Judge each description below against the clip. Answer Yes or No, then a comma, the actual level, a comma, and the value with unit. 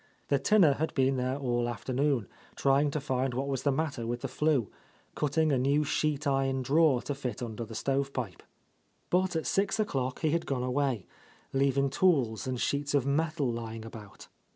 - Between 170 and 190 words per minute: Yes, average, 185 wpm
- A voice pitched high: No, low, 135 Hz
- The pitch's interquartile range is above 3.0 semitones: No, average, 2.7 semitones